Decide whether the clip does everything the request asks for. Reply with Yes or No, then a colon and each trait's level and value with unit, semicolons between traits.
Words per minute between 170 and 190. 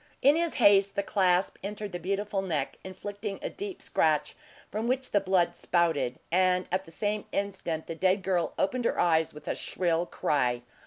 Yes: average, 180 wpm